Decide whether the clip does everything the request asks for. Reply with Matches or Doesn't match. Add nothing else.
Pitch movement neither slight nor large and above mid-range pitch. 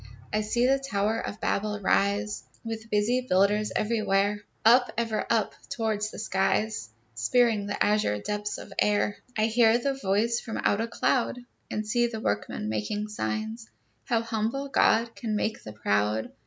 Doesn't match